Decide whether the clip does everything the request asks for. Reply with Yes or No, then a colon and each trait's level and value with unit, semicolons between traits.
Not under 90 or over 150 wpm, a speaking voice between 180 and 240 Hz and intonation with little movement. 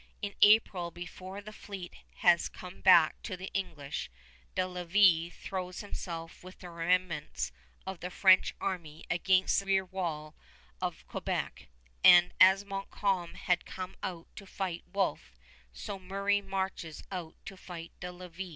Yes: average, 145 wpm; medium, 185 Hz; narrow, 2.0 semitones